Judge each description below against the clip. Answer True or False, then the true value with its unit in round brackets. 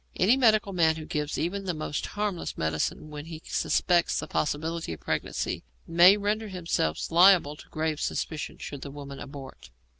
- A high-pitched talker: False (160 Hz)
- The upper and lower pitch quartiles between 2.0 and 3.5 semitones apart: False (4.2 semitones)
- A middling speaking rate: True (170 wpm)